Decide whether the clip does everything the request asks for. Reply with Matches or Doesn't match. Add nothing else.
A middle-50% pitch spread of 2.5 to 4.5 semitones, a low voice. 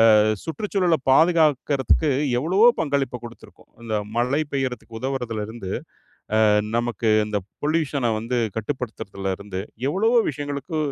Doesn't match